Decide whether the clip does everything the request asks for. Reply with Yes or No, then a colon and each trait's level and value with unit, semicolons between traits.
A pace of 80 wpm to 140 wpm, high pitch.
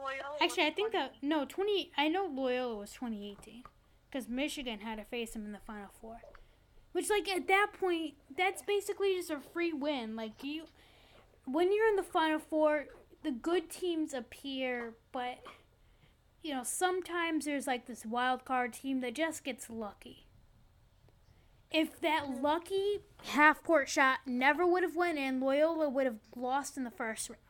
No: average, 170 wpm; very high, 290 Hz